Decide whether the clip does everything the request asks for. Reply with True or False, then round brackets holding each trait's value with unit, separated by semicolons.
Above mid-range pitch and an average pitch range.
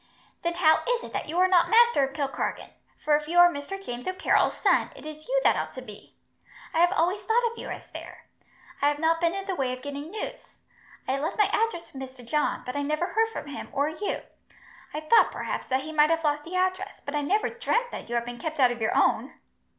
True (315 Hz; 5.0 semitones)